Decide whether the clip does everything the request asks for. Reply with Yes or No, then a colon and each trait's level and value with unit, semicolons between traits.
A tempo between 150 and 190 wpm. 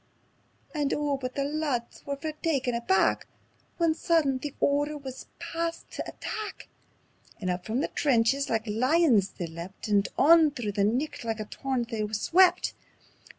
Yes: average, 165 wpm